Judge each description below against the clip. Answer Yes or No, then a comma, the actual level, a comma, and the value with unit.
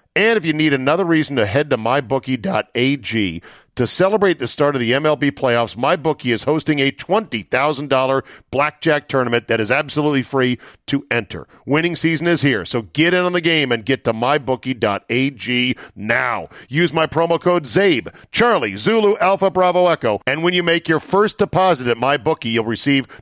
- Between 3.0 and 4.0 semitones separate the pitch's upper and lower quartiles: No, average, 4.9 semitones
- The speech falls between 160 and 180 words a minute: Yes, average, 175 wpm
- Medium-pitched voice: Yes, medium, 145 Hz